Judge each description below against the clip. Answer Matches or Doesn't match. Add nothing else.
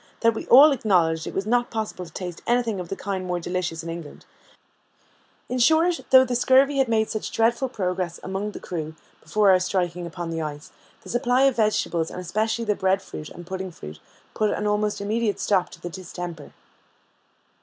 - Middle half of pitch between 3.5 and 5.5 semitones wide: Matches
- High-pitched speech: Matches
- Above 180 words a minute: Matches